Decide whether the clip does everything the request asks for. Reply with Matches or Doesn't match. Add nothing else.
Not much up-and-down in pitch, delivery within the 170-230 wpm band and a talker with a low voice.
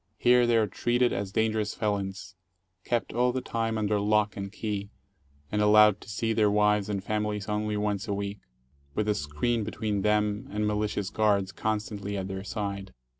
Matches